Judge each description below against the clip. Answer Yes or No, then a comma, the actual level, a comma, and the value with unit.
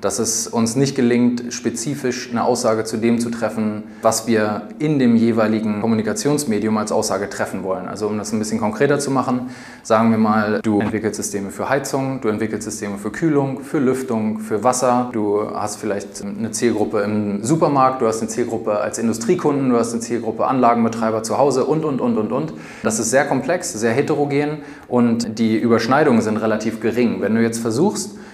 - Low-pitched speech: Yes, low, 115 Hz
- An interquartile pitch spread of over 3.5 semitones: No, average, 2.7 semitones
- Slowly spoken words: No, average, 185 wpm